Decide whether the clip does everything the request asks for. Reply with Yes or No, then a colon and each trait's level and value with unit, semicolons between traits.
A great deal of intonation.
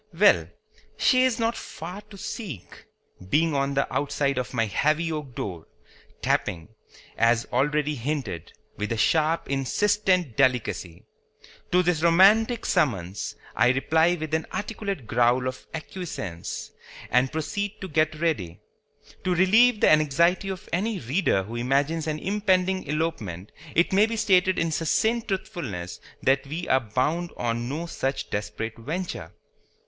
Yes: wide, 6.8 semitones